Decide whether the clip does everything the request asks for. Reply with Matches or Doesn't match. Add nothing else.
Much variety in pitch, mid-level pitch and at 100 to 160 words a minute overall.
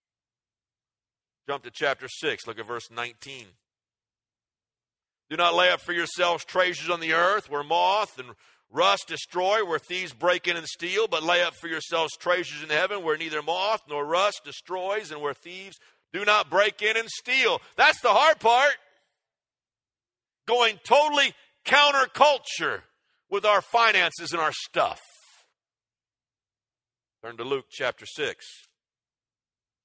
Matches